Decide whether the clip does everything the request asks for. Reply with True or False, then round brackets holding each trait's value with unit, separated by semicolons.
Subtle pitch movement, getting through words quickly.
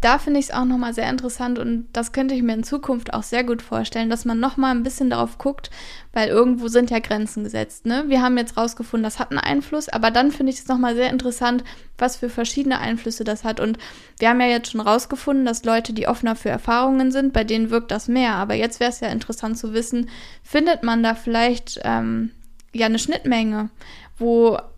True (1.9 semitones; 230 wpm)